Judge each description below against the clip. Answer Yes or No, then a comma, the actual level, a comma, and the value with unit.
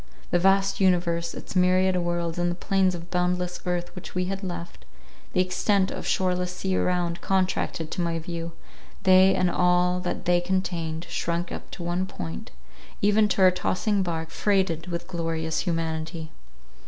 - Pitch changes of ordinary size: No, narrow, 1.7 semitones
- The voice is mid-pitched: Yes, medium, 180 Hz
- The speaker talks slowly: No, average, 155 wpm